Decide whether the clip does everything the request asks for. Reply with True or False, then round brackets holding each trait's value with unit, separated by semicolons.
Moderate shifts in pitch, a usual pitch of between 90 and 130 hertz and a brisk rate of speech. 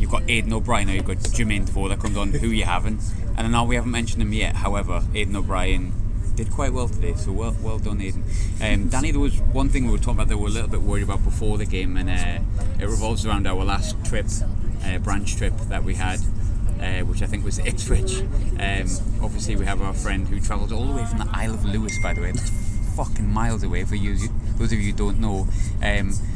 False (1.8 semitones; 100 Hz; 250 wpm)